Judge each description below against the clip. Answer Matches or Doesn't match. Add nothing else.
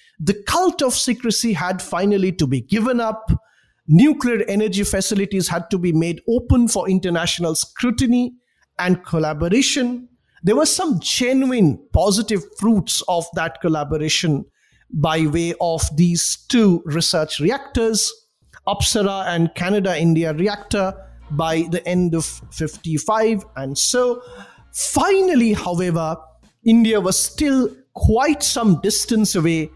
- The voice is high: Matches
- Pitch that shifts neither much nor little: Doesn't match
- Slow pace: Matches